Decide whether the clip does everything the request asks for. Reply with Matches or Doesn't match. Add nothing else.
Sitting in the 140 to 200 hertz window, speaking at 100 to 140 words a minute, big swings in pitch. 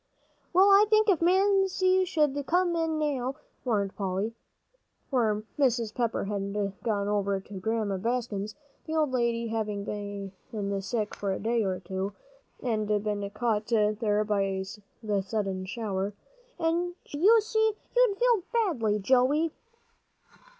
Doesn't match